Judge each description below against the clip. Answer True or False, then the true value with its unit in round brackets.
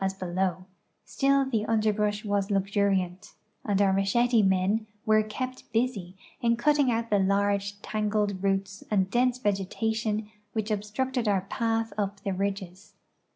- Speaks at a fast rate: False (140 wpm)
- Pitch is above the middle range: True (205 Hz)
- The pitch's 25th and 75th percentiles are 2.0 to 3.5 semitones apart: True (2.5 semitones)